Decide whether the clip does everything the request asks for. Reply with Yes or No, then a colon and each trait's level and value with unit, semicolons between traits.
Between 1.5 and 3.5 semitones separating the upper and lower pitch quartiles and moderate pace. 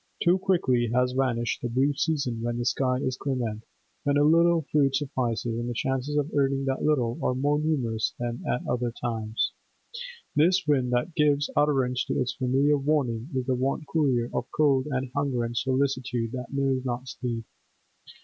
Yes: average, 2.9 semitones; average, 180 wpm